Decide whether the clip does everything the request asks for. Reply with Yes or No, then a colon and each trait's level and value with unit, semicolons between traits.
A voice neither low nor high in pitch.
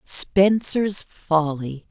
Yes: medium, 175 Hz